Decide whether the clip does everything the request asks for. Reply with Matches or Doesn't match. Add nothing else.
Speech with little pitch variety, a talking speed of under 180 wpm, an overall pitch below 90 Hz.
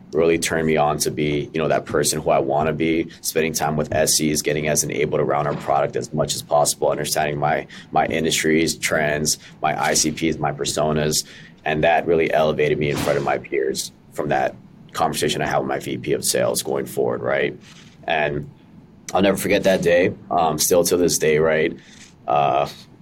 Doesn't match